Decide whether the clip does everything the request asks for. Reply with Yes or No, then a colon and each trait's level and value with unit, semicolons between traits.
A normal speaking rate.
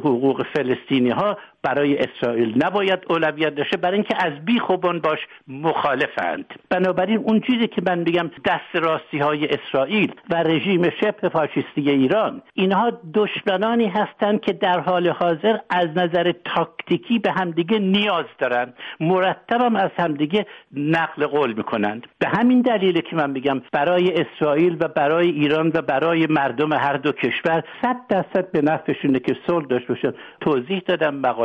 Yes: average, 145 wpm